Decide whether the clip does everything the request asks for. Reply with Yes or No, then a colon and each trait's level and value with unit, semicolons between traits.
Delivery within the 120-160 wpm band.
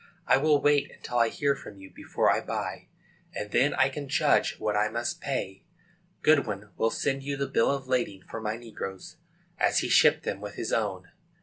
No: average, 200 wpm